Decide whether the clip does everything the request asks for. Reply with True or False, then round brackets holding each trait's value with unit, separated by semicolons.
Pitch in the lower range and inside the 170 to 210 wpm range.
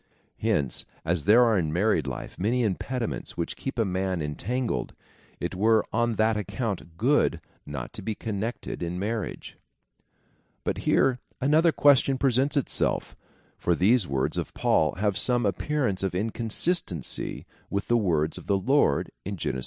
False (105 Hz; 160 wpm)